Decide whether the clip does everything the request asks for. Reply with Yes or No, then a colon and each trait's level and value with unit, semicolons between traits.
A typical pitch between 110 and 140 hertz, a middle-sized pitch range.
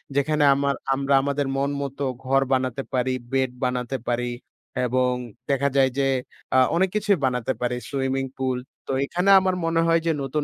No: low, 135 Hz; narrow, 1.8 semitones